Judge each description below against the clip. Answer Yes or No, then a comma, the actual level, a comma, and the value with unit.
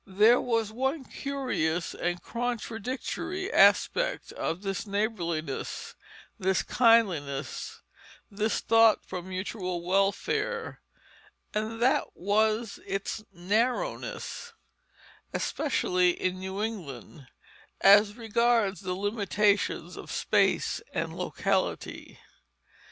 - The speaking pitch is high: Yes, high, 210 Hz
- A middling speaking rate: No, slow, 90 wpm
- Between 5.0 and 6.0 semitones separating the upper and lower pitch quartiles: No, average, 4.0 semitones